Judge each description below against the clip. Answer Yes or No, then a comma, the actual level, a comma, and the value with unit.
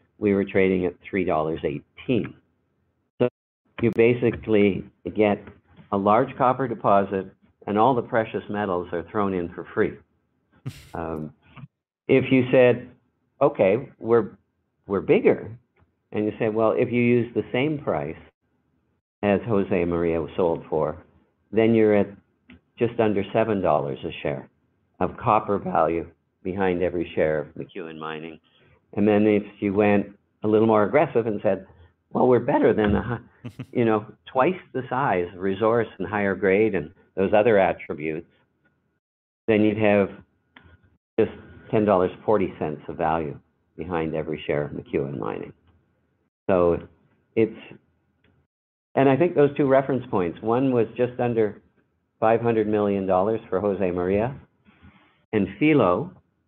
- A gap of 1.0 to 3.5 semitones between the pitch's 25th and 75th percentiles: No, average, 4.2 semitones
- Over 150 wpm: No, average, 140 wpm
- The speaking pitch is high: No, low, 105 Hz